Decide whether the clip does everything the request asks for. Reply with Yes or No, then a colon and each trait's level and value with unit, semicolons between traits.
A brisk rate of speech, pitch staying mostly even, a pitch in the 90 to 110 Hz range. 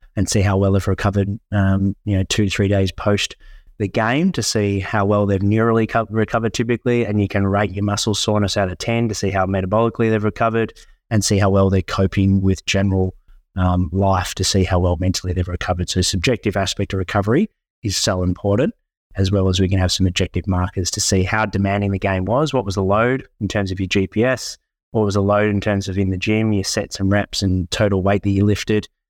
Yes: fast, 225 wpm; narrow, 1.9 semitones; low, 100 Hz